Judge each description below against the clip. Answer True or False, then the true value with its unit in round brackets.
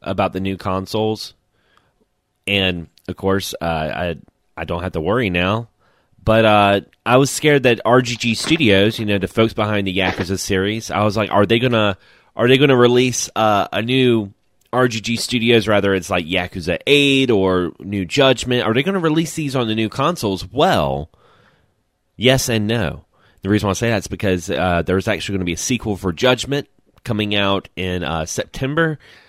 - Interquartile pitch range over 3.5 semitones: True (4.6 semitones)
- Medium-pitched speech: False (105 Hz)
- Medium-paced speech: True (180 wpm)